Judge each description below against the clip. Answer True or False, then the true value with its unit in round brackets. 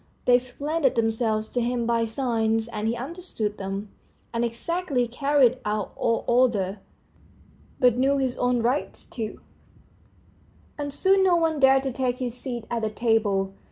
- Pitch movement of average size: True (3.1 semitones)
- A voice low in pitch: False (245 Hz)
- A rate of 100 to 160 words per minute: True (155 wpm)